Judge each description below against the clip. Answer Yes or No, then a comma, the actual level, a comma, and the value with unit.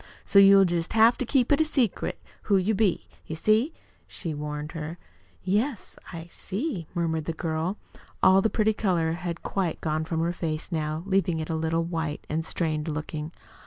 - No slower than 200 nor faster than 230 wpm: No, average, 180 wpm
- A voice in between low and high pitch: Yes, medium, 170 Hz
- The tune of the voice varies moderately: Yes, average, 3.8 semitones